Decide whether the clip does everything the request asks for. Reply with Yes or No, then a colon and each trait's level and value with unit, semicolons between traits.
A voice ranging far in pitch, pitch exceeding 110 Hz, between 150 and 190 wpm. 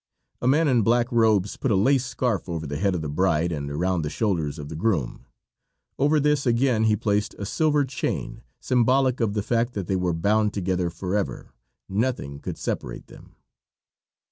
No: wide, 5.8 semitones; low, 105 Hz; average, 185 wpm